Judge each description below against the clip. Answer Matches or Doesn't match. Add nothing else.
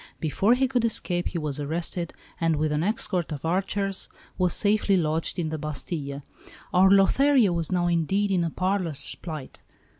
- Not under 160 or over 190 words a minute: Matches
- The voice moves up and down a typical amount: Matches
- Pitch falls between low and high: Matches